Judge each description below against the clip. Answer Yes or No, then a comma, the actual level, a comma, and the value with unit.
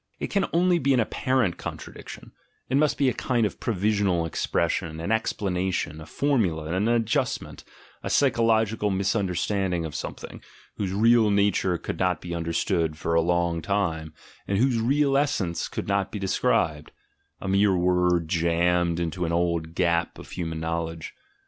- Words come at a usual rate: Yes, average, 155 wpm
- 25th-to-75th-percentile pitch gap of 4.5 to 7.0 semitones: Yes, average, 5.0 semitones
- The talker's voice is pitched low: Yes, very low, 95 Hz